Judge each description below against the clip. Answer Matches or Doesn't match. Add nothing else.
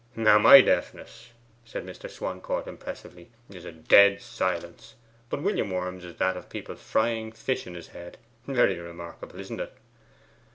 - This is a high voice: Doesn't match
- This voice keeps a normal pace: Matches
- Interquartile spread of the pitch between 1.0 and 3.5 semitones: Doesn't match